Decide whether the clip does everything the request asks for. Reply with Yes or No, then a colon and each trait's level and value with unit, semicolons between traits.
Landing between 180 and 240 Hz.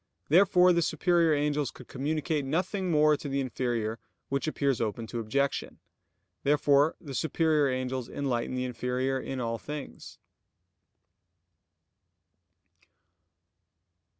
No: medium, 140 Hz